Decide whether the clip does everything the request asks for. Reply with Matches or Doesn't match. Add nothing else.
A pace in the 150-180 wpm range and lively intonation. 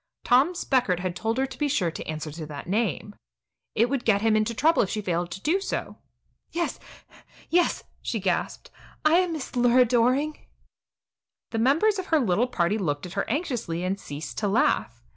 Doesn't match